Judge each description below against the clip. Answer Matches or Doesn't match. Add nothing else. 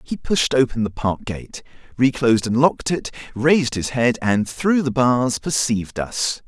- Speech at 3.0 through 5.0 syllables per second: Matches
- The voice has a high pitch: Doesn't match